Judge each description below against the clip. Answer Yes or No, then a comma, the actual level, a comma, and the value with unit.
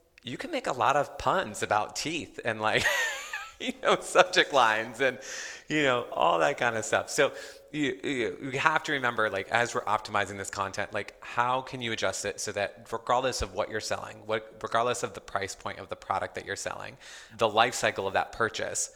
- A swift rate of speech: Yes, fast, 210 wpm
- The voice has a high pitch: No, low, 120 Hz